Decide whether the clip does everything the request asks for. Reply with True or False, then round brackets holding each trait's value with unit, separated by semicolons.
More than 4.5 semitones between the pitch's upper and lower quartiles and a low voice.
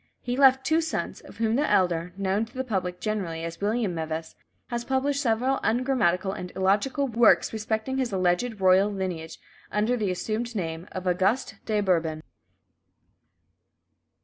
False (5.2 semitones; 210 Hz)